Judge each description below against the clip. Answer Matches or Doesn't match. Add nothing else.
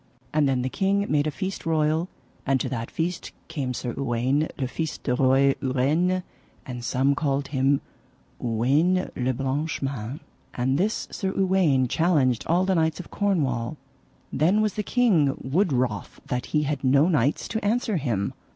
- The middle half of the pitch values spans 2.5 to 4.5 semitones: Doesn't match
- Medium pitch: Matches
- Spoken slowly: Doesn't match